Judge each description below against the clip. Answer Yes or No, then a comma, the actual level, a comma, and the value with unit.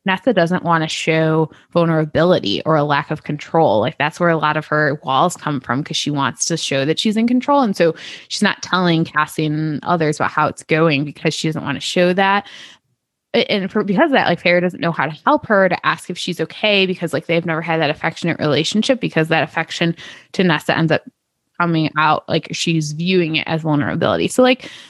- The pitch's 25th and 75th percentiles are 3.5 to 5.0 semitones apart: No, average, 2.7 semitones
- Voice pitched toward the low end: No, medium, 160 Hz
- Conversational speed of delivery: No, fast, 220 wpm